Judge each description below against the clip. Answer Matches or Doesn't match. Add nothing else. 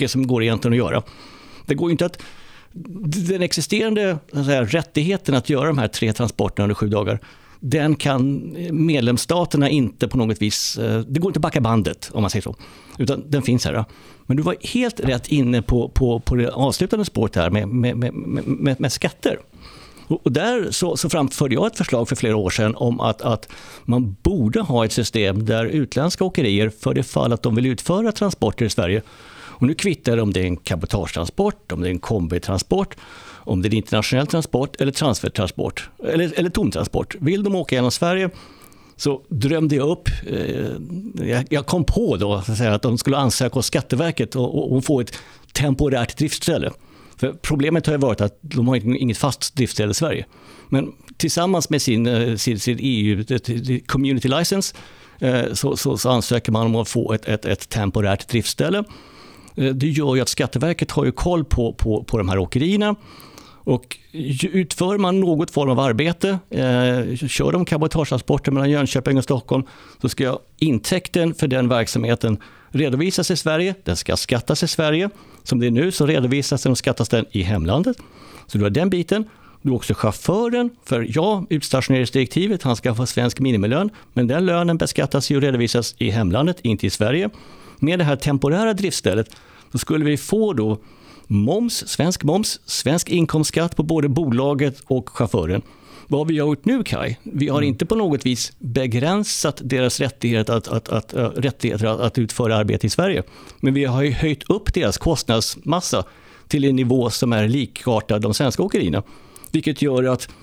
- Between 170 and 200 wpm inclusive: Matches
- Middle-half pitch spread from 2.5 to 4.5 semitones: Doesn't match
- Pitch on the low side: Matches